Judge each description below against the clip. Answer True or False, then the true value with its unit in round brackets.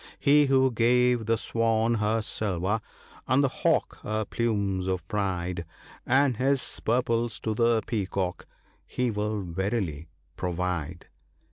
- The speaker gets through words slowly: True (130 wpm)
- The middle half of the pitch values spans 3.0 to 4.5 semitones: True (4.1 semitones)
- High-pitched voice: False (110 Hz)